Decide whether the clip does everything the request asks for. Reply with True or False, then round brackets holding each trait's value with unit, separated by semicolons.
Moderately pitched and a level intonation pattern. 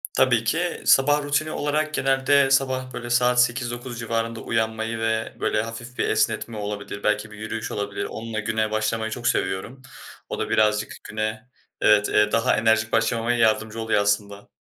False (115 Hz; 2.3 semitones)